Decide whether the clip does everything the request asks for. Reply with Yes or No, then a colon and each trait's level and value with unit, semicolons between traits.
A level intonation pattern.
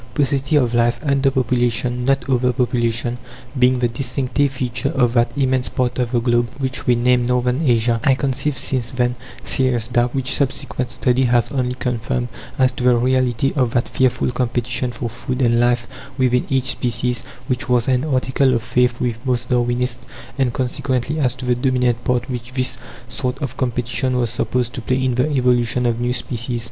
Yes: narrow, 1.3 semitones